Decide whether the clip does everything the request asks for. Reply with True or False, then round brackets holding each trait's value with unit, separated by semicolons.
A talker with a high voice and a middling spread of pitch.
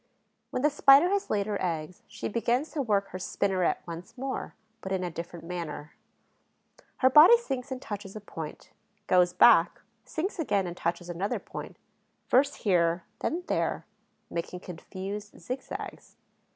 False (200 Hz; 6.8 semitones)